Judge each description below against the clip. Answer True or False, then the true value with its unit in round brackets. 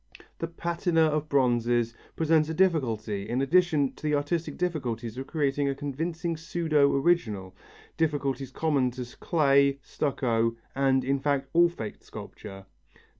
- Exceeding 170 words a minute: False (135 wpm)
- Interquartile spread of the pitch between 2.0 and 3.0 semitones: False (4.2 semitones)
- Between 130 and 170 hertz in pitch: True (140 Hz)